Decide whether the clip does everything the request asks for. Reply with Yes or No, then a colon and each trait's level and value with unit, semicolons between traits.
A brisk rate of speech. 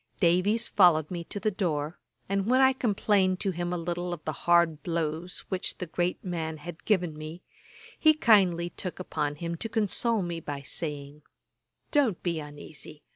No: average, 175 wpm